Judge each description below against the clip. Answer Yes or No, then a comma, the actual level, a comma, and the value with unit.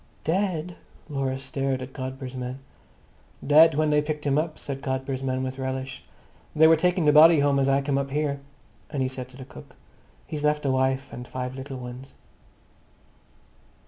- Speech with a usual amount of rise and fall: No, narrow, 2.2 semitones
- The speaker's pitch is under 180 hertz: Yes, low, 135 Hz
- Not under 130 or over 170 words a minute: No, average, 180 wpm